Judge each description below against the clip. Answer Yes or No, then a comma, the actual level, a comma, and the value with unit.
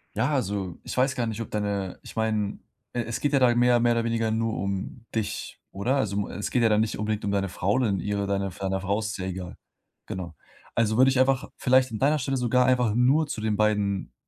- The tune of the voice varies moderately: Yes, average, 3.7 semitones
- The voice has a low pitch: Yes, low, 110 Hz